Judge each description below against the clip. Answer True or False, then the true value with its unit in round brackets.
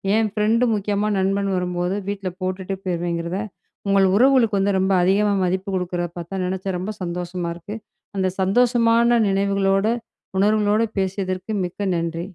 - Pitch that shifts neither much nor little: False (2.3 semitones)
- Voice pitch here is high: True (195 Hz)